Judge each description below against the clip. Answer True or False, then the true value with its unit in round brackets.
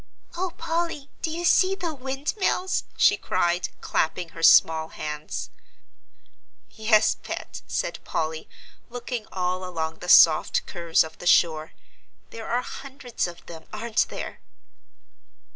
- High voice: True (215 Hz)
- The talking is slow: True (125 wpm)